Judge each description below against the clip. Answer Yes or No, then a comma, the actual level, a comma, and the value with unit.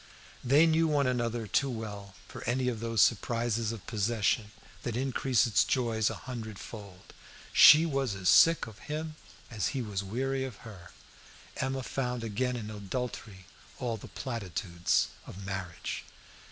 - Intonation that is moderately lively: Yes, average, 3.9 semitones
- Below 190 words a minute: Yes, average, 155 wpm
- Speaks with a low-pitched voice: Yes, low, 115 Hz